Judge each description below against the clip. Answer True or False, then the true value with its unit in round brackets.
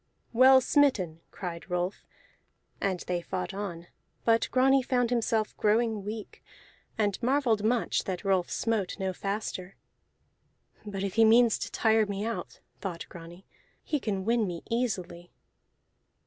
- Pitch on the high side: True (210 Hz)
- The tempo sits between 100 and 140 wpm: True (135 wpm)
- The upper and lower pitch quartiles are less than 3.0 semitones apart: False (3.9 semitones)